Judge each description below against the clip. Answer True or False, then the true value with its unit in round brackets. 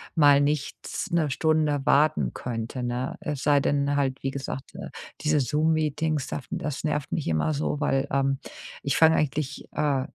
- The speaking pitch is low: False (145 Hz)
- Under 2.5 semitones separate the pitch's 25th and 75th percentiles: True (2.1 semitones)